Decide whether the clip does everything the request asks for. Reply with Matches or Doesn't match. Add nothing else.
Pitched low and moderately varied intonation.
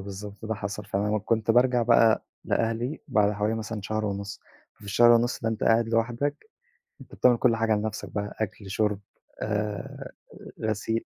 Doesn't match